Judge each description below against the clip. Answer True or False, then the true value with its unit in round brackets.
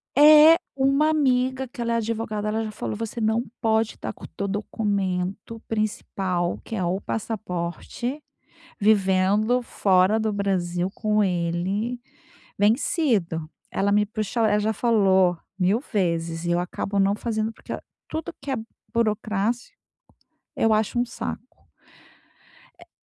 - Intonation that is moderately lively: True (3.4 semitones)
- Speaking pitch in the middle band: False (215 Hz)